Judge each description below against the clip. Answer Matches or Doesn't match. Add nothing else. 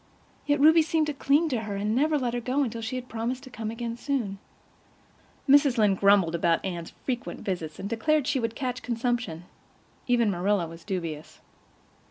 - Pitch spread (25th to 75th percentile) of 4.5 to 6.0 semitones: Matches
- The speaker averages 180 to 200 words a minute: Matches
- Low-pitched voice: Doesn't match